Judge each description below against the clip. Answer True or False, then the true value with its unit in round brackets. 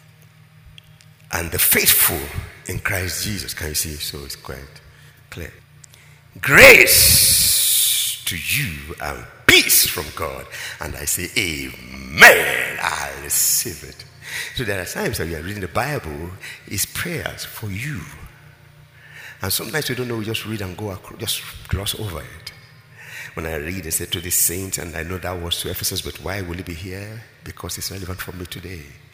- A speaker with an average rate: True (175 wpm)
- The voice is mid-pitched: False (95 Hz)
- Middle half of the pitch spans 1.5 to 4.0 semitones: False (5.5 semitones)